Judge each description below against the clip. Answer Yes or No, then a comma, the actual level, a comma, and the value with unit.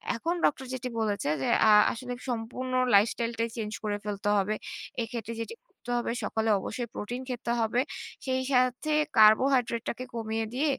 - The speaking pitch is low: No, high, 230 Hz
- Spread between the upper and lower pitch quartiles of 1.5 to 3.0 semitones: Yes, narrow, 2.5 semitones